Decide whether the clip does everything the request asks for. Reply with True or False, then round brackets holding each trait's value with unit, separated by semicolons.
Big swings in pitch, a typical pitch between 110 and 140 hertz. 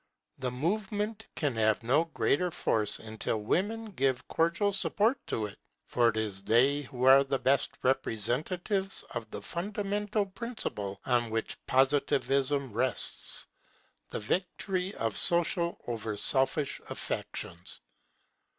True (8.6 semitones; 135 Hz)